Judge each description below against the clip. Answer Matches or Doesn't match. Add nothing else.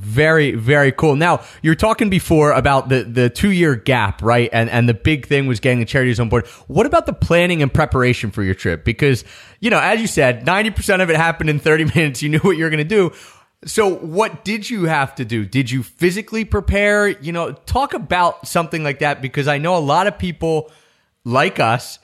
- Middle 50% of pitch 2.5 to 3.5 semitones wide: Doesn't match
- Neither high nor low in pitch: Matches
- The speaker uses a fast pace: Matches